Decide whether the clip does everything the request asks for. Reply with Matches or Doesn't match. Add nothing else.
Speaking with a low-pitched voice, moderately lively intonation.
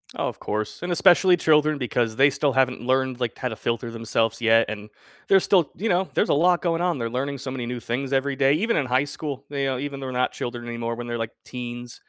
Matches